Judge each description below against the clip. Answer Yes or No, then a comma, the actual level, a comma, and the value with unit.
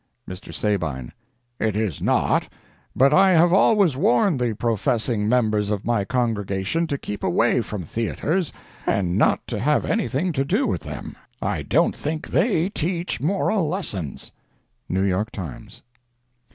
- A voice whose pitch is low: Yes, low, 120 Hz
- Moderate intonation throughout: No, wide, 7.9 semitones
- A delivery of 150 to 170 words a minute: No, average, 140 wpm